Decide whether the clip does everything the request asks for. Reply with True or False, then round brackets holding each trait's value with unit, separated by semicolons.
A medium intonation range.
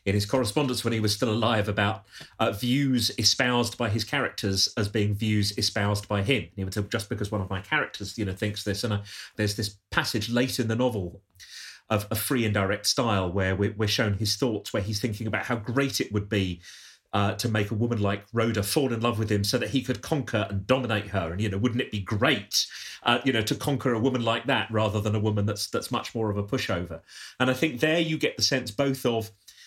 True (3.4 semitones)